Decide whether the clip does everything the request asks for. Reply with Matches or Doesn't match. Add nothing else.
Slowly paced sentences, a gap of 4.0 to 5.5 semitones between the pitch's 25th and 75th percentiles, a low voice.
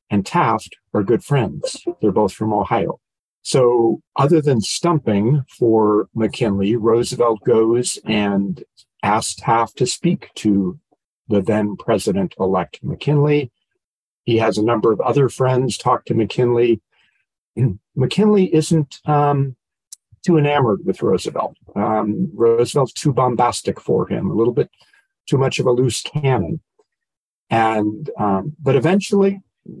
Matches